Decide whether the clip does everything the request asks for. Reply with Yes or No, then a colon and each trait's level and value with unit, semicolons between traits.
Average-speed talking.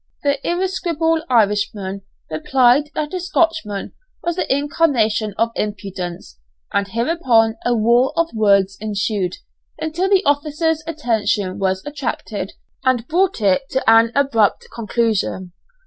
No: slow, 120 wpm